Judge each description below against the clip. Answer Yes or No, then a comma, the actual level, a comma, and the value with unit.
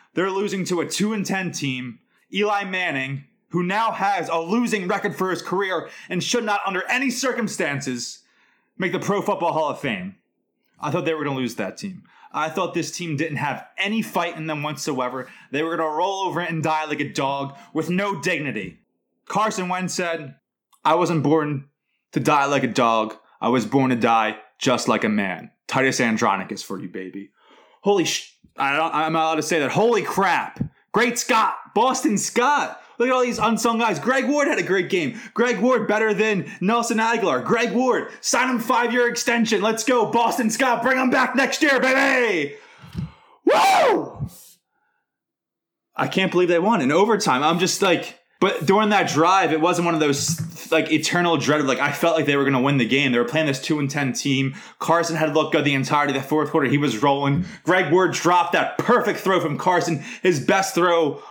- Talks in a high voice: No, medium, 175 Hz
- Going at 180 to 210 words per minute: Yes, average, 200 wpm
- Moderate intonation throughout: No, wide, 6.2 semitones